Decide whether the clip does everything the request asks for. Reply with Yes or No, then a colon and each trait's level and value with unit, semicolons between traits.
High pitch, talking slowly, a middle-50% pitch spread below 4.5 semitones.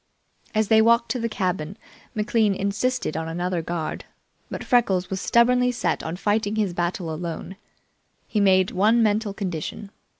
No: high, 200 Hz; average, 155 wpm; average, 3.8 semitones